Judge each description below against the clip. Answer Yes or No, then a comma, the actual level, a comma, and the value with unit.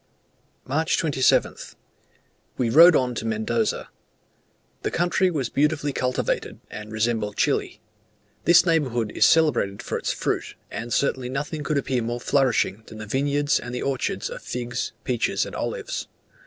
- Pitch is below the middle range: Yes, low, 130 Hz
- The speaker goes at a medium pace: Yes, average, 145 wpm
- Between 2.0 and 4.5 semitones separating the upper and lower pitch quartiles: Yes, average, 4.1 semitones